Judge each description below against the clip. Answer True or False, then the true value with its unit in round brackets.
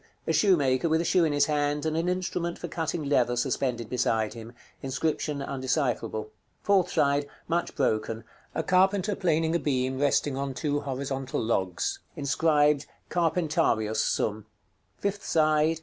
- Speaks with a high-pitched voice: False (145 Hz)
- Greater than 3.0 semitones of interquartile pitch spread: True (4.1 semitones)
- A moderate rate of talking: True (150 wpm)